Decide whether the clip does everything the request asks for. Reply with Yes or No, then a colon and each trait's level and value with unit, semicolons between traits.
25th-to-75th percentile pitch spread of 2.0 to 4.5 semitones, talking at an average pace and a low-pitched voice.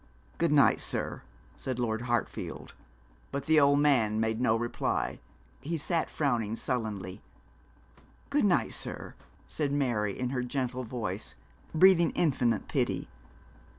No: average, 4.1 semitones; slow, 125 wpm; low, 125 Hz